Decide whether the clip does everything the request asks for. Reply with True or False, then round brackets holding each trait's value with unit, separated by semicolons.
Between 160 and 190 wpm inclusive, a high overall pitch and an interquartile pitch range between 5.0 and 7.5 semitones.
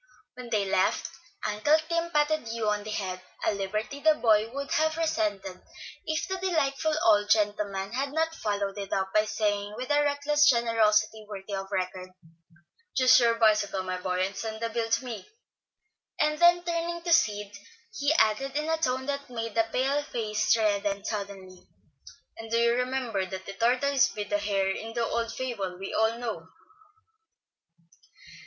True (170 wpm; 225 Hz; 5.4 semitones)